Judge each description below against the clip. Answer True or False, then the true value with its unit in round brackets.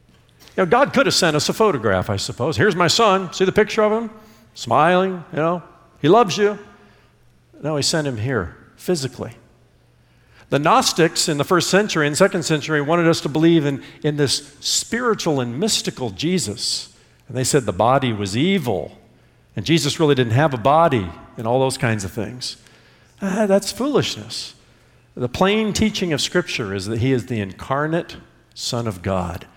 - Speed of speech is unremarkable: True (180 wpm)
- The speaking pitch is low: False (145 Hz)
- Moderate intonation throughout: False (7.4 semitones)